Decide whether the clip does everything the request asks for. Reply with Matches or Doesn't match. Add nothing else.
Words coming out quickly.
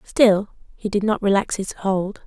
Doesn't match